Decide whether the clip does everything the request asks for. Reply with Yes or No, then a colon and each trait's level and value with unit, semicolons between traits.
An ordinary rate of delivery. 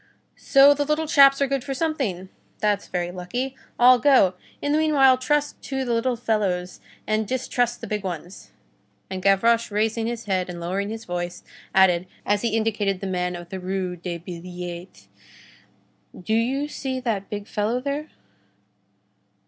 Yes: average, 165 wpm